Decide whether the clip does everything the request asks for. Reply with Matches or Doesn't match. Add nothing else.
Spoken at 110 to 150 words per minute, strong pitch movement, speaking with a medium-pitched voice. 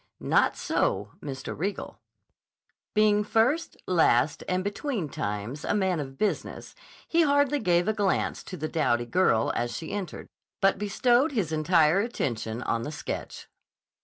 Matches